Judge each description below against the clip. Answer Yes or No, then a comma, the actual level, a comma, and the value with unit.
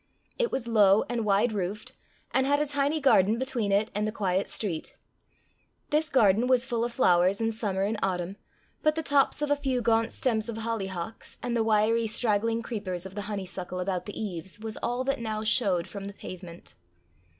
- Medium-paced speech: Yes, average, 195 wpm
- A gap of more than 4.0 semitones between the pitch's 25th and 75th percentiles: No, average, 3.7 semitones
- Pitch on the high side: Yes, high, 220 Hz